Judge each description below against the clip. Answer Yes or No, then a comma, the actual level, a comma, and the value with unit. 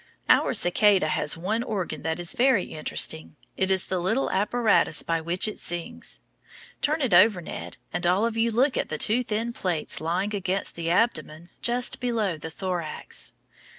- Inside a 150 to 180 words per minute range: Yes, average, 175 wpm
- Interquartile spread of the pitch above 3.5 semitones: Yes, average, 5.1 semitones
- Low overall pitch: No, high, 190 Hz